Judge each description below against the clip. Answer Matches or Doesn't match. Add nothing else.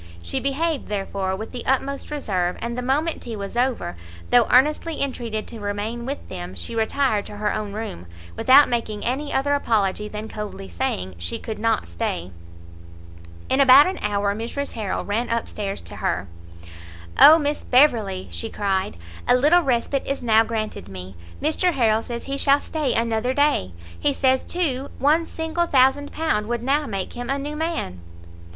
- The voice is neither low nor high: Doesn't match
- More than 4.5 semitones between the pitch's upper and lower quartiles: Matches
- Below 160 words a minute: Doesn't match